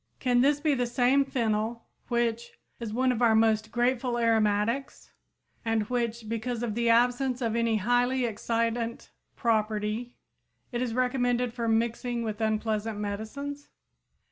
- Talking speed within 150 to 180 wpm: No, slow, 135 wpm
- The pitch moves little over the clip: Yes, narrow, 1.9 semitones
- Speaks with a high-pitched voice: Yes, high, 235 Hz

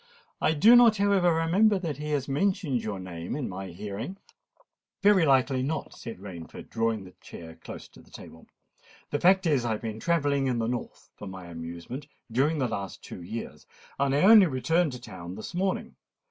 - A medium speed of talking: Yes, average, 190 wpm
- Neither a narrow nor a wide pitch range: No, wide, 8.5 semitones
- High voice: No, low, 135 Hz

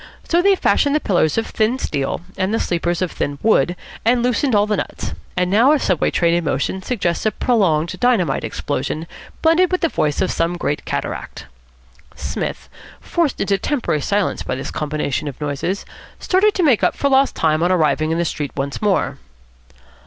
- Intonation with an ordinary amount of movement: No, wide, 8.1 semitones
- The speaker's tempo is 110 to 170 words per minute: No, average, 190 wpm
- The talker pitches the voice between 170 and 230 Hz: Yes, medium, 185 Hz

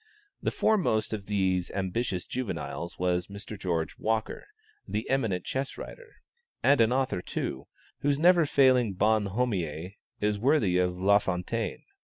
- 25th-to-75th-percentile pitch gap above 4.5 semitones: Yes, wide, 5.6 semitones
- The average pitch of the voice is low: Yes, low, 105 Hz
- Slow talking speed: Yes, slow, 130 wpm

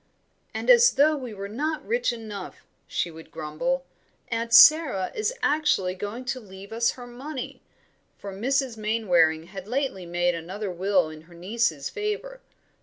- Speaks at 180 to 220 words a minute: No, average, 155 wpm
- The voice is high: Yes, high, 220 Hz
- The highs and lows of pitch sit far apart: Yes, wide, 6.7 semitones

